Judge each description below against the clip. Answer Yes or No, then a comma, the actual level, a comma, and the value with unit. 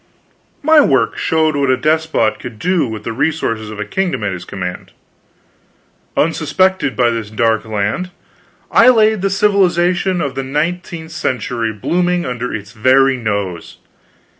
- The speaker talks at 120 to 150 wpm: Yes, average, 145 wpm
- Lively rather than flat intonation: Yes, wide, 8.0 semitones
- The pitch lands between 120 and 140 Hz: Yes, low, 135 Hz